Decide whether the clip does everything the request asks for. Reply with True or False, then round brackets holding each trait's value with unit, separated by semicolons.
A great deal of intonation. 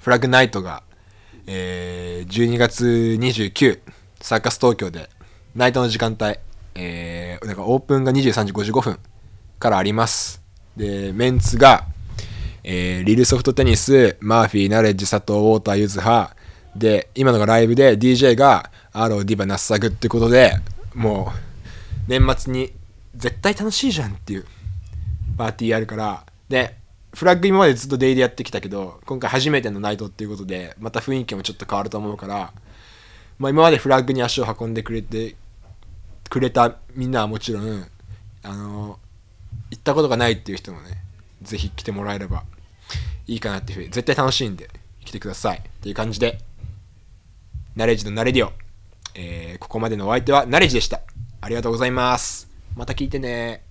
False (3.6 semitones)